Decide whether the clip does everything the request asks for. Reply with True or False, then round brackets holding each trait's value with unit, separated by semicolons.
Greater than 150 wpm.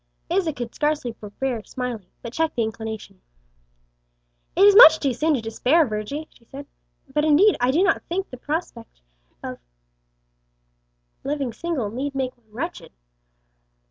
False (145 wpm)